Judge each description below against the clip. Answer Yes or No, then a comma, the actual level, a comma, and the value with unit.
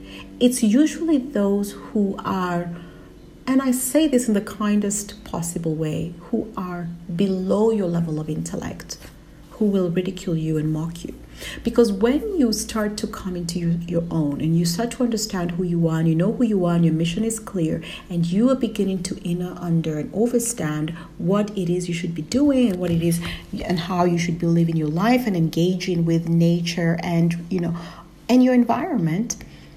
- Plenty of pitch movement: No, average, 4.4 semitones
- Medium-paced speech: Yes, average, 190 wpm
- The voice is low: No, medium, 180 Hz